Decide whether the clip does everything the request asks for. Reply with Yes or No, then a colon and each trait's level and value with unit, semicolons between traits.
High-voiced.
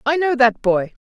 Yes: high, 245 Hz